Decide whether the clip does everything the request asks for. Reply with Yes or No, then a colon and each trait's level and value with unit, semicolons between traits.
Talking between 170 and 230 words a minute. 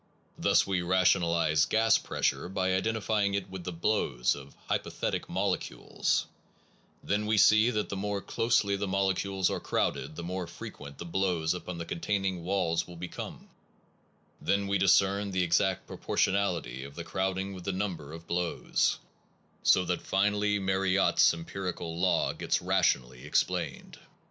No: average, 155 wpm